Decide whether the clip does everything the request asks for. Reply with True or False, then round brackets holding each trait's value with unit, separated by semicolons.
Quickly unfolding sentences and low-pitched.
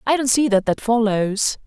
False (215 wpm; 230 Hz)